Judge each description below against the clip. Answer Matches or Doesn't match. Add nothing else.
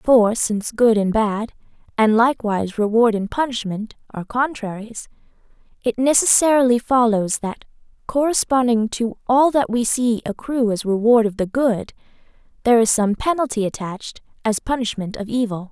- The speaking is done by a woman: Matches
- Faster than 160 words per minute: Doesn't match